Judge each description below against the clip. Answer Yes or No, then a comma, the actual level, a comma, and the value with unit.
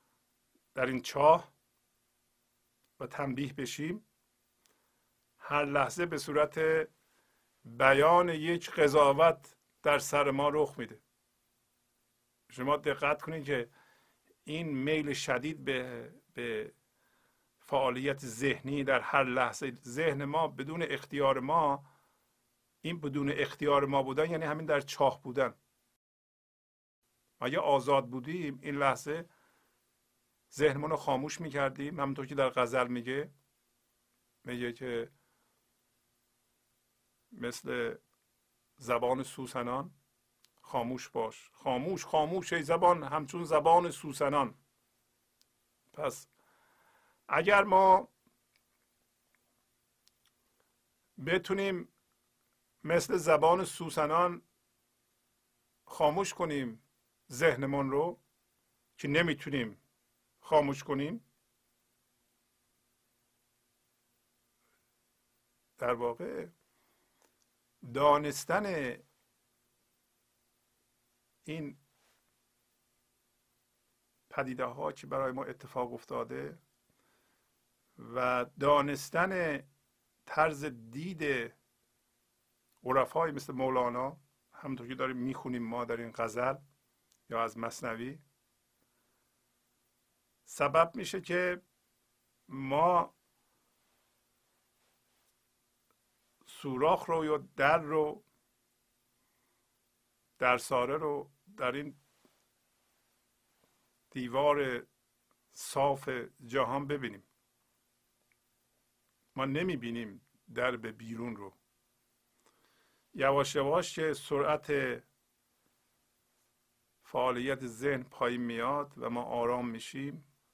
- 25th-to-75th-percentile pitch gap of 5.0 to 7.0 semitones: No, average, 3.9 semitones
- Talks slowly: Yes, slow, 75 wpm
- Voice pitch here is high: No, medium, 140 Hz